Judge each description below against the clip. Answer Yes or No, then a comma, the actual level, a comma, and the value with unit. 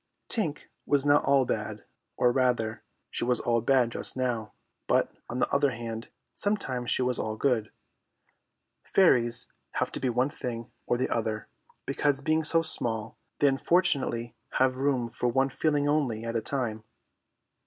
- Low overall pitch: Yes, low, 125 Hz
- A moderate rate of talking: Yes, average, 160 wpm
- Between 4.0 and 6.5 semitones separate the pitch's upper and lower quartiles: No, average, 3.2 semitones